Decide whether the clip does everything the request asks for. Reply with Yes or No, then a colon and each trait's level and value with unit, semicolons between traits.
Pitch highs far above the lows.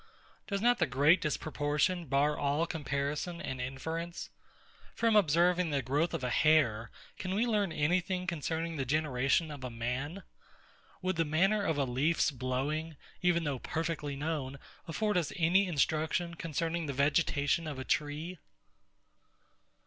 No: average, 3.4 semitones